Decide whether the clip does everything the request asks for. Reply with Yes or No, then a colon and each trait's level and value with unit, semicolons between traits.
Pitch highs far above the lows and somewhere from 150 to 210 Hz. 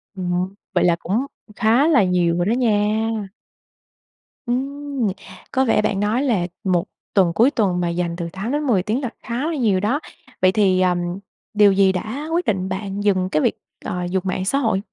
No: average, 4.8 semitones; high, 205 Hz